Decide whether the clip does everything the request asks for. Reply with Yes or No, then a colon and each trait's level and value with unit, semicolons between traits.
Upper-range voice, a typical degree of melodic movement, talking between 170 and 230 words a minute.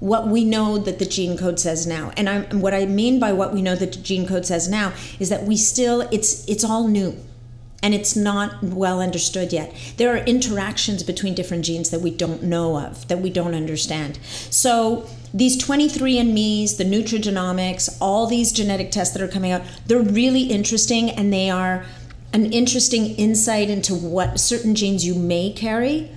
Yes: high, 195 Hz; average, 3.7 semitones; average, 185 wpm